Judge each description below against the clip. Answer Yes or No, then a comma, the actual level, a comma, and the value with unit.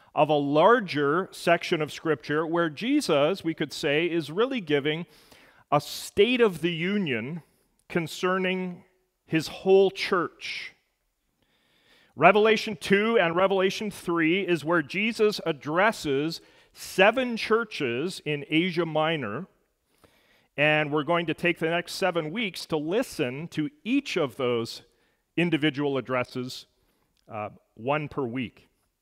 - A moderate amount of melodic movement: Yes, average, 4.2 semitones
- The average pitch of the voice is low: No, medium, 170 Hz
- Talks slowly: Yes, slow, 120 wpm